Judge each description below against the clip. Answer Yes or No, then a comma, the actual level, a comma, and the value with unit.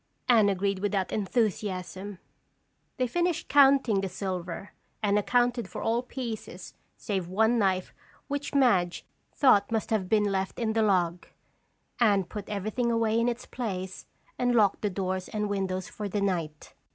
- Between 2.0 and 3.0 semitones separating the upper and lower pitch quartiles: No, average, 3.7 semitones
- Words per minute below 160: Yes, average, 150 wpm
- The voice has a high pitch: Yes, high, 205 Hz